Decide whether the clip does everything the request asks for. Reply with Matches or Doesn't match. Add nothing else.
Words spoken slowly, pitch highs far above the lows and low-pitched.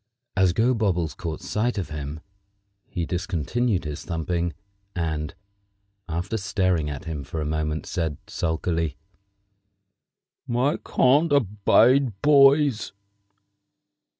Matches